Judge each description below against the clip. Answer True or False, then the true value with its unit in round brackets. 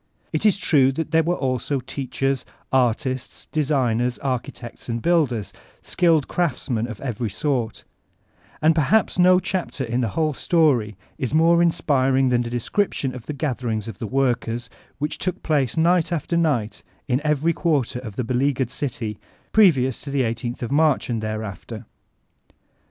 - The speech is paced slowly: False (155 wpm)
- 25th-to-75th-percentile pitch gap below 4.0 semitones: False (4.7 semitones)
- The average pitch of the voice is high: False (135 Hz)